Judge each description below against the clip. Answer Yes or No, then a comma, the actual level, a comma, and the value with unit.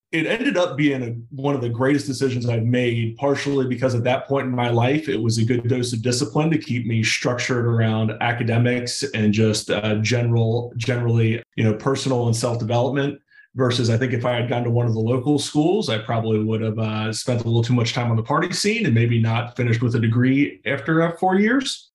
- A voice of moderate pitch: No, low, 120 Hz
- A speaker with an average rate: No, fast, 225 wpm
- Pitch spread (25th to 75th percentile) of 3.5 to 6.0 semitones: No, average, 3.0 semitones